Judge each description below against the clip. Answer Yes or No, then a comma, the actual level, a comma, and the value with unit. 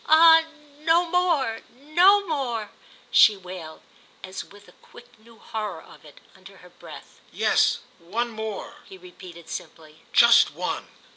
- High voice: Yes, high, 220 Hz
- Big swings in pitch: Yes, wide, 8.4 semitones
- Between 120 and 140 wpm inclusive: Yes, slow, 135 wpm